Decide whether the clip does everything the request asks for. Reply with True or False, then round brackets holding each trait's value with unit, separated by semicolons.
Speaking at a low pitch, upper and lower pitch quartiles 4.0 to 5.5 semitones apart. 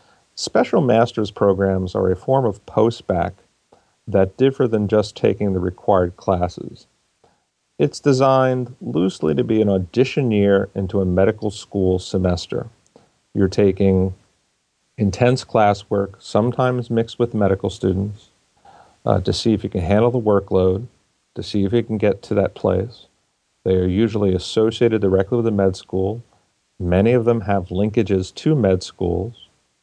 False (100 Hz; 3.3 semitones)